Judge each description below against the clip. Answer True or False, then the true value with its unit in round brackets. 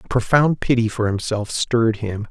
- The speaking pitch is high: False (115 Hz)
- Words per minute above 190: False (180 wpm)